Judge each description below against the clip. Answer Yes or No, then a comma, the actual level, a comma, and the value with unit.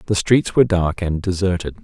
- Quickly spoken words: No, average, 195 wpm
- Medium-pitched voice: No, very low, 95 Hz